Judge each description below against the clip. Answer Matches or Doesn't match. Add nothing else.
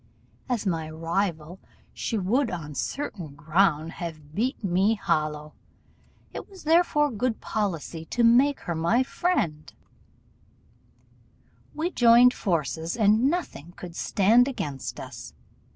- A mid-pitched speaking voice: Doesn't match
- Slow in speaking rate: Matches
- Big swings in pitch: Matches